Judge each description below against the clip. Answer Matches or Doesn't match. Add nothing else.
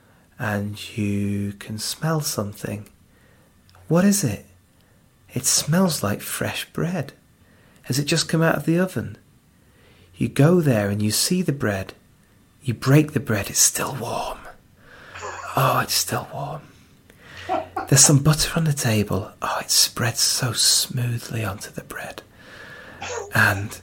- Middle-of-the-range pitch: Doesn't match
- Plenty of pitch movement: Matches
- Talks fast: Doesn't match